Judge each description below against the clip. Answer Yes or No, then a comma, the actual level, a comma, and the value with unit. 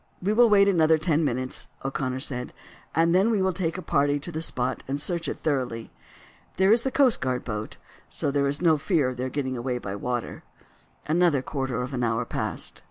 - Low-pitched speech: No, medium, 145 Hz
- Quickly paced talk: Yes, fast, 210 wpm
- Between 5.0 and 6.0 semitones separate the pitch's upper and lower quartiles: Yes, average, 5.3 semitones